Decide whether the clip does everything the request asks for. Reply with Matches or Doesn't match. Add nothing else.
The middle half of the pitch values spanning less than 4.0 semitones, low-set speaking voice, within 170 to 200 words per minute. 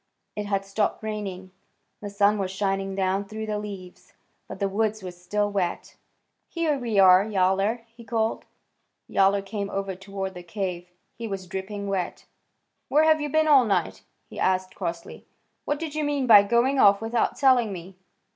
Doesn't match